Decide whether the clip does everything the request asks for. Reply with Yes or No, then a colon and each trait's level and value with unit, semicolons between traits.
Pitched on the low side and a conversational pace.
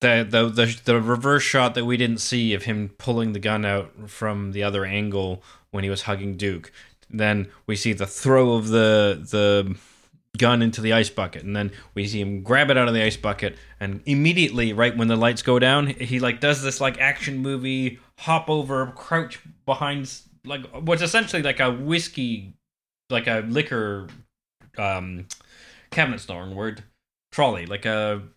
Yes: low, 115 Hz; average, 180 wpm